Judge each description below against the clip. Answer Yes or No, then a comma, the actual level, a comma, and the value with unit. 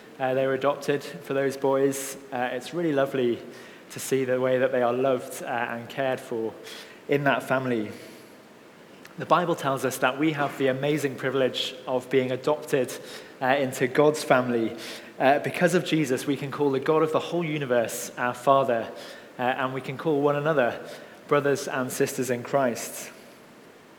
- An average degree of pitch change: No, narrow, 2.0 semitones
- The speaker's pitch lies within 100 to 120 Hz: No, low, 135 Hz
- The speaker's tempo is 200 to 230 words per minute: No, average, 175 wpm